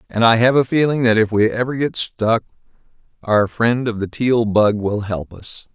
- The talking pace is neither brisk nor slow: No, fast, 210 wpm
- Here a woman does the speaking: No, male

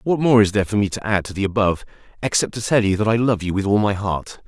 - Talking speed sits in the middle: No, fast, 310 wpm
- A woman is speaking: No, male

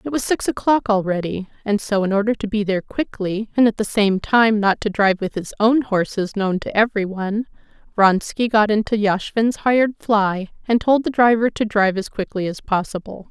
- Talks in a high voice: Yes, high, 210 Hz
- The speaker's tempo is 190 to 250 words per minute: Yes, average, 200 wpm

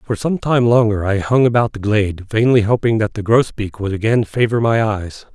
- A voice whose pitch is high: No, low, 110 Hz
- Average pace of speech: No, fast, 215 wpm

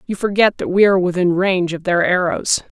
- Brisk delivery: Yes, fast, 215 wpm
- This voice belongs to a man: No, female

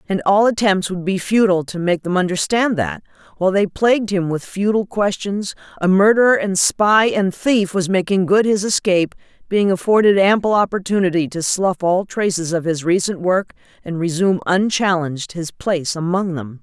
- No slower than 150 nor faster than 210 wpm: Yes, average, 175 wpm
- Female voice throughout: Yes, female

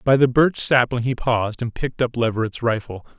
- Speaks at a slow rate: No, fast, 205 wpm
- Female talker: No, male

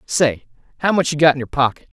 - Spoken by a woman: No, male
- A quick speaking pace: Yes, fast, 240 wpm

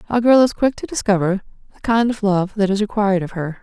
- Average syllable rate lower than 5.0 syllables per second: No, 6.1 syllables/s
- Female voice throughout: Yes, female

